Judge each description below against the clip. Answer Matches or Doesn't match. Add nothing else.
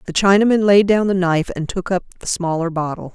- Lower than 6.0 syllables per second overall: Doesn't match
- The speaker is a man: Doesn't match